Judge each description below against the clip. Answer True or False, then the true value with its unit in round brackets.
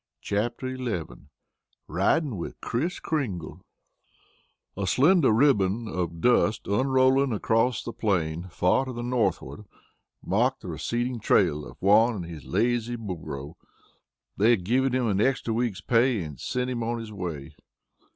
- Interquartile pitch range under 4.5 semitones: False (5.5 semitones)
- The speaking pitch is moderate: False (115 Hz)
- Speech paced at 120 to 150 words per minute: True (140 wpm)